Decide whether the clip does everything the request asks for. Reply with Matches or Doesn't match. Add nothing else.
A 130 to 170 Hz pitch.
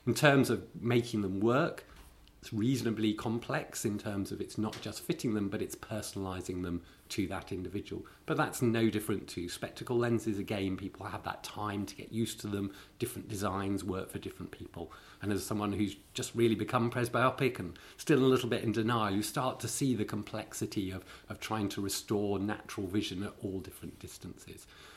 Doesn't match